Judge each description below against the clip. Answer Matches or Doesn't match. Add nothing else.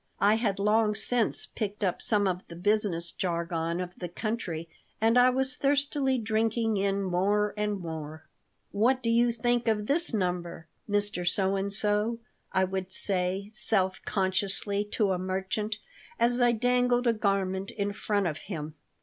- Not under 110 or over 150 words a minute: Doesn't match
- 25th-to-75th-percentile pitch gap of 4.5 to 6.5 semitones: Doesn't match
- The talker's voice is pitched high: Matches